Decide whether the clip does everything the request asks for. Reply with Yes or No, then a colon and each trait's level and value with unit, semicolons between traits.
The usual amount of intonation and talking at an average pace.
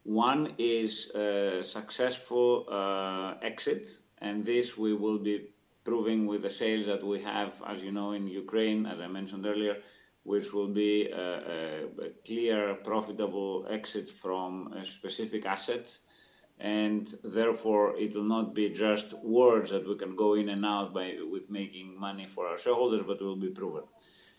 No: narrow, 1.7 semitones; average, 165 wpm